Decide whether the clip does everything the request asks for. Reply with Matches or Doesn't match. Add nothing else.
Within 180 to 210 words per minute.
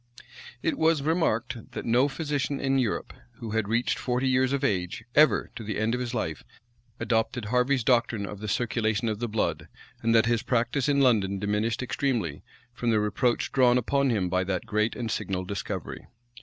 Matches